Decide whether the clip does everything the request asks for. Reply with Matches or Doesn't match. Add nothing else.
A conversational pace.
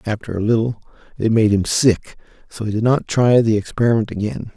Matches